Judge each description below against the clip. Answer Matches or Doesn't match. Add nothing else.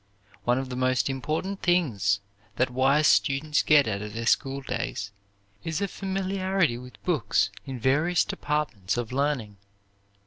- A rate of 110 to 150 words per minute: Matches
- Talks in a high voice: Doesn't match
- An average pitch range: Matches